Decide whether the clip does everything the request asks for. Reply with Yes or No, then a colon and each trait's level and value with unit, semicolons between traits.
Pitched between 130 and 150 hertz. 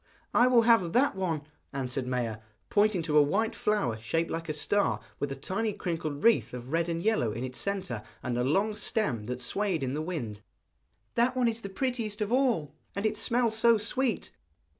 No: medium, 185 Hz